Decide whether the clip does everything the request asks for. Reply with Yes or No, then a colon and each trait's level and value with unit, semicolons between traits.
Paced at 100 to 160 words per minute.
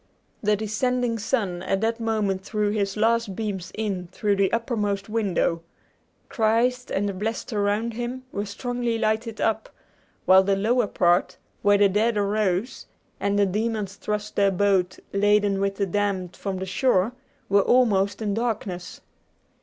Yes: average, 155 wpm